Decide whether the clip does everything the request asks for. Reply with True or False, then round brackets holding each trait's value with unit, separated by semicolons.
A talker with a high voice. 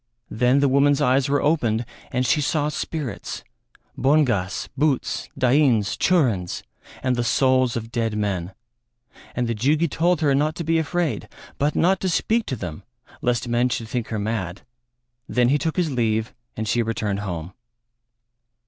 False (125 Hz)